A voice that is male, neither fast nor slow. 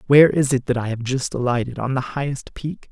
No: male; fast, 225 wpm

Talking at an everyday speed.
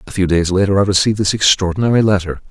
No: fast, 215 wpm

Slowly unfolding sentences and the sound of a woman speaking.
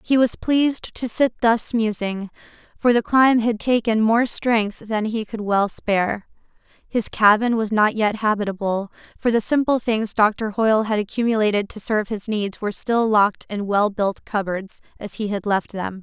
No: average, 185 wpm; female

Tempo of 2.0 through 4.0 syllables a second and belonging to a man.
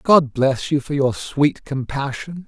Yes: 3.8 syllables/s; male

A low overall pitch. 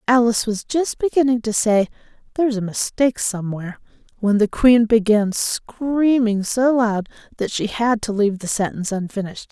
No: high, 225 Hz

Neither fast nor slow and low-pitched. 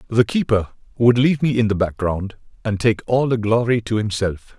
Yes: average, 195 wpm; low, 115 Hz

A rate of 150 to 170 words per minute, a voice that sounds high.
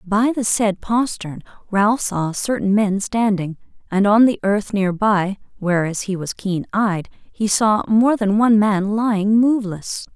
Yes: average, 165 wpm; high, 205 Hz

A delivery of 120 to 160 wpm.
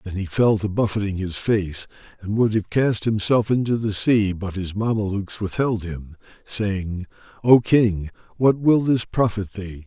No: average, 170 wpm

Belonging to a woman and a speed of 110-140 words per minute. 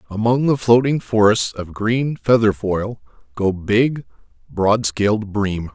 No: male; slow, 135 wpm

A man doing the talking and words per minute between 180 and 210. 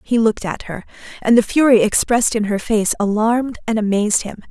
No: female; average, 200 wpm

